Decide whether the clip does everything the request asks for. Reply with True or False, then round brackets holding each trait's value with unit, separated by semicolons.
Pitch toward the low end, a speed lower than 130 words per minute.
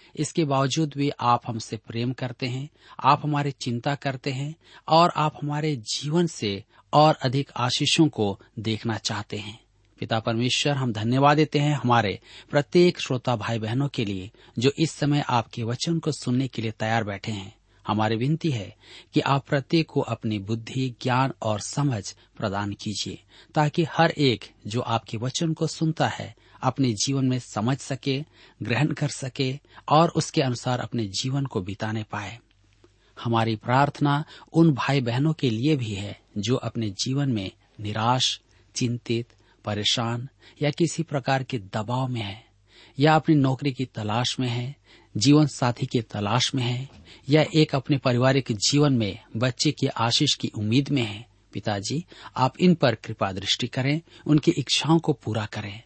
False (125 Hz; 160 wpm)